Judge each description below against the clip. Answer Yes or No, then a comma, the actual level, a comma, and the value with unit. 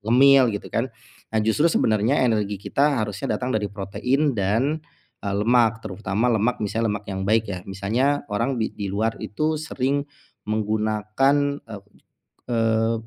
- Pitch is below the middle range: Yes, low, 110 Hz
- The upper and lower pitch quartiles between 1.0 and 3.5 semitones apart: No, average, 4.0 semitones